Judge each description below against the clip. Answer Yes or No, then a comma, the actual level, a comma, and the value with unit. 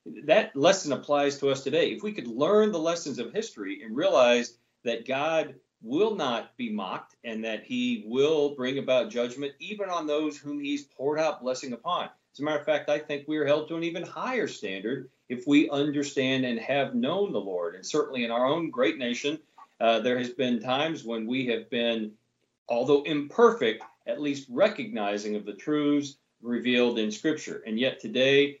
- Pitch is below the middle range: No, medium, 145 Hz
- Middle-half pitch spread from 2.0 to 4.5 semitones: No, average, 5.2 semitones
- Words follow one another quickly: No, average, 190 wpm